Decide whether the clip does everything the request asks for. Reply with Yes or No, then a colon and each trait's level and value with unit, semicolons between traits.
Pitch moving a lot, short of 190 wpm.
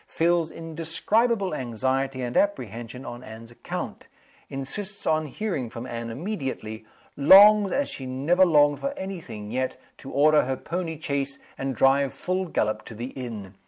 Yes: wide, 6.1 semitones; average, 155 wpm